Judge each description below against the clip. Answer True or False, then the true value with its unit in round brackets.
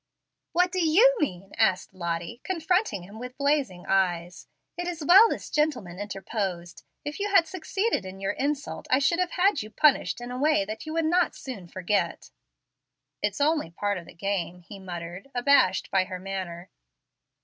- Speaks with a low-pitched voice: False (220 Hz)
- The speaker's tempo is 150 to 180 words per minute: True (175 wpm)